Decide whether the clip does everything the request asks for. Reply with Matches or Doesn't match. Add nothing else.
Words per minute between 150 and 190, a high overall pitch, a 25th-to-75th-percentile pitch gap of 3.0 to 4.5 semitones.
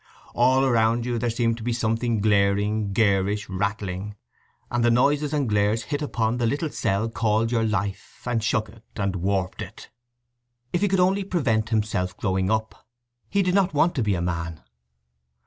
Doesn't match